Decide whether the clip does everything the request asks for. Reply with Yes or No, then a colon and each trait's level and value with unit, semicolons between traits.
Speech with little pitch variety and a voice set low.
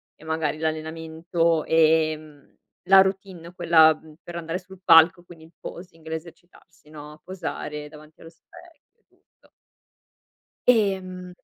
No: narrow, 2.3 semitones; medium, 165 Hz